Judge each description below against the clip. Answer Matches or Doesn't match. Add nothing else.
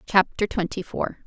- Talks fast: Doesn't match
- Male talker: Doesn't match